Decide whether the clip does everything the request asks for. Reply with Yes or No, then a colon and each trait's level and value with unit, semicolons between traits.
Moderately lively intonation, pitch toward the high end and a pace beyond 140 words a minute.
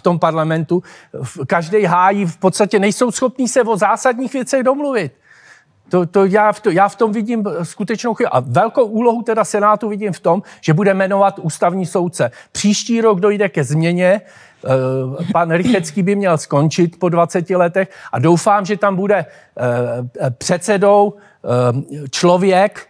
Yes: average, 3.8 semitones; high, 195 Hz; average, 150 wpm